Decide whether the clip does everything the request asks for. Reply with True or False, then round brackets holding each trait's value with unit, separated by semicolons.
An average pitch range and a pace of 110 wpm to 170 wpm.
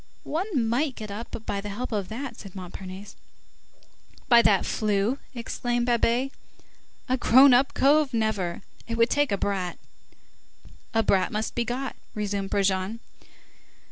True (3.9 semitones; 140 wpm)